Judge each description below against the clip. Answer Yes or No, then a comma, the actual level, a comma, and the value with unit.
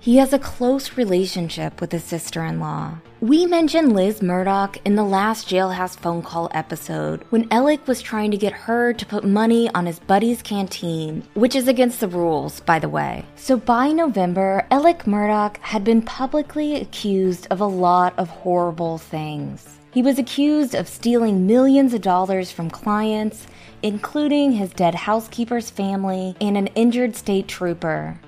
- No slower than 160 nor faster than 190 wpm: Yes, average, 165 wpm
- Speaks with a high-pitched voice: Yes, high, 205 Hz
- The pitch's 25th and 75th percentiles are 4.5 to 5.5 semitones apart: Yes, average, 5.2 semitones